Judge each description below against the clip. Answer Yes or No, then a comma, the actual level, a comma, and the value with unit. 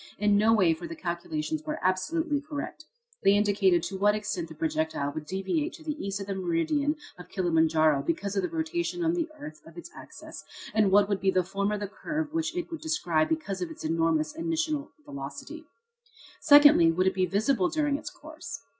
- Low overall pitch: No, high, 200 Hz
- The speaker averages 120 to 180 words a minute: No, average, 200 wpm